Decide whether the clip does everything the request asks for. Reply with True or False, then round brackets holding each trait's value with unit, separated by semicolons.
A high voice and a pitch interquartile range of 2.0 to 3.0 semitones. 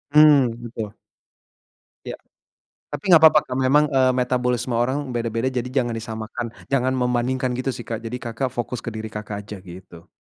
False (125 Hz; 2.4 semitones)